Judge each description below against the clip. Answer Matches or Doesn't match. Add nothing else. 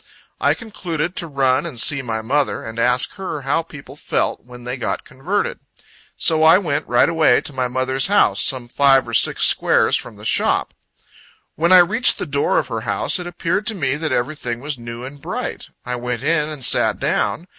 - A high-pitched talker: Doesn't match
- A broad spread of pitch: Doesn't match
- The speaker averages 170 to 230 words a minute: Matches